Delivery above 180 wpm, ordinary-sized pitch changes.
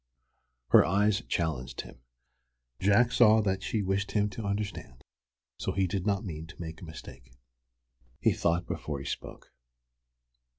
No: average, 155 wpm; average, 4.1 semitones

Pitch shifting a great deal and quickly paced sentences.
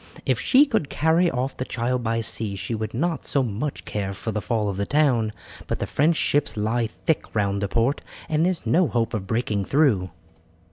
Yes: wide, 5.7 semitones; fast, 215 wpm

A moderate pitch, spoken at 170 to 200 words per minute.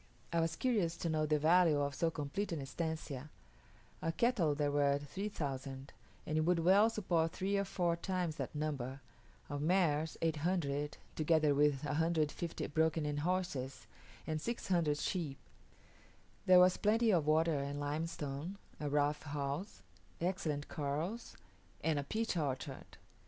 No: medium, 155 Hz; average, 145 wpm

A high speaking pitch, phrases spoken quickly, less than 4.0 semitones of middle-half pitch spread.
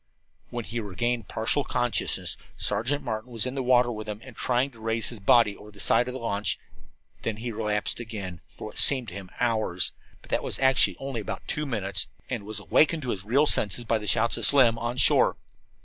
No: low, 115 Hz; fast, 215 wpm; average, 2.8 semitones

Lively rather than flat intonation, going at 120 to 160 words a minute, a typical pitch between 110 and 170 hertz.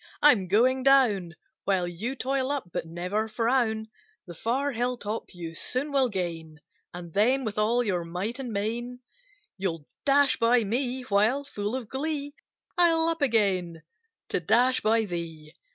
No: wide, 6.1 semitones; average, 155 wpm; high, 225 Hz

